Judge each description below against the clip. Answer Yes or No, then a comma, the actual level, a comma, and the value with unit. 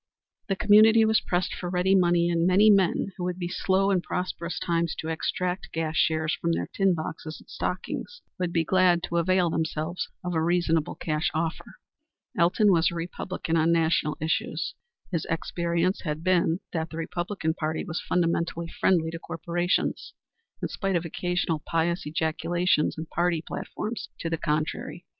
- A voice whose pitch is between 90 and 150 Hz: No, medium, 170 Hz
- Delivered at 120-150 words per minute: No, average, 165 wpm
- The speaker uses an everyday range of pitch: No, narrow, 2.0 semitones